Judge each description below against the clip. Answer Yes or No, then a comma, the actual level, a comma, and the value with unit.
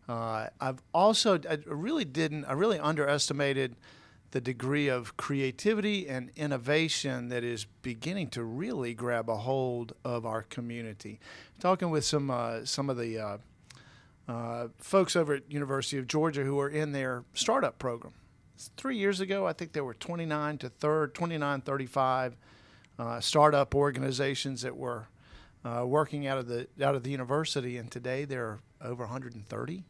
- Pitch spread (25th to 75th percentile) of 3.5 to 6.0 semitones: Yes, average, 3.9 semitones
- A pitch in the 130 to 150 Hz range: Yes, low, 135 Hz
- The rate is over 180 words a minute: No, average, 160 wpm